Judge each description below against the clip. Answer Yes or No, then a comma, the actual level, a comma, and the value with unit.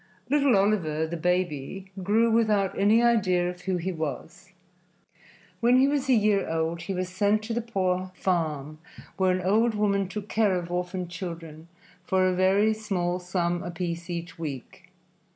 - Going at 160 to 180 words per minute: Yes, average, 165 wpm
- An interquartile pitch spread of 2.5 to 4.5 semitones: Yes, average, 3.3 semitones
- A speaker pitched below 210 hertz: Yes, medium, 185 Hz